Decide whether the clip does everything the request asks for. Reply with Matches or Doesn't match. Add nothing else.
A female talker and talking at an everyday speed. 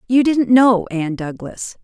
Matches